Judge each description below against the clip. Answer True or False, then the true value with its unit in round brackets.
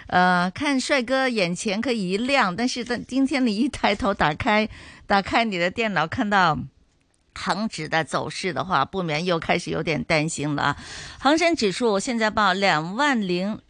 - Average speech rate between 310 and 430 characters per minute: False (245 characters per minute)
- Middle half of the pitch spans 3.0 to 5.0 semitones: False (5.4 semitones)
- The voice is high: True (200 Hz)